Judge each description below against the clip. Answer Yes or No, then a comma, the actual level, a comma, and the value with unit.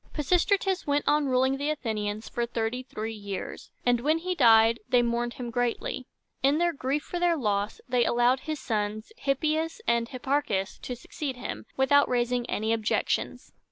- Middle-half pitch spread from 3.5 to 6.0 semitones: Yes, average, 4.2 semitones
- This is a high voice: Yes, very high, 250 Hz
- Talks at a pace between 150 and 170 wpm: No, average, 180 wpm